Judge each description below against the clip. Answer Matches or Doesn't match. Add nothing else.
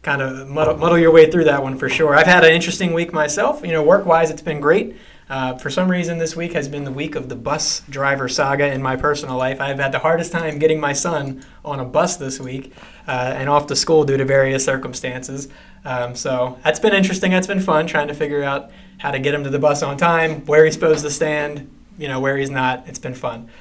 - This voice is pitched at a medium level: Matches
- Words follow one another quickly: Matches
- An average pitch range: Matches